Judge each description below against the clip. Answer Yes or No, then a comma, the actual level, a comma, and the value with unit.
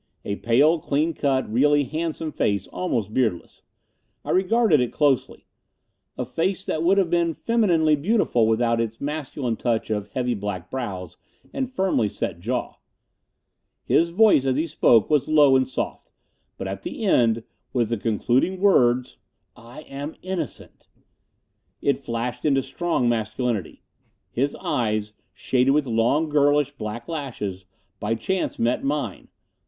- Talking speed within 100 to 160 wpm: Yes, average, 140 wpm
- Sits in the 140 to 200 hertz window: No, low, 130 Hz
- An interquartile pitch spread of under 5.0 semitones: No, wide, 5.4 semitones